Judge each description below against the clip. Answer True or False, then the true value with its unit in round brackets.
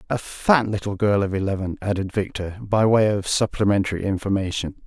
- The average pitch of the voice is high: False (100 Hz)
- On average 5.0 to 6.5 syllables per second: True (5.5 syllables/s)